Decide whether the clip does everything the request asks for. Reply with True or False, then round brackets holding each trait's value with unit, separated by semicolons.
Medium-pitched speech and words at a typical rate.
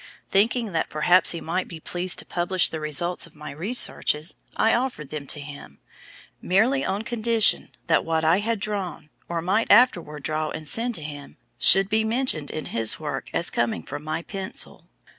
True (175 Hz; 180 wpm)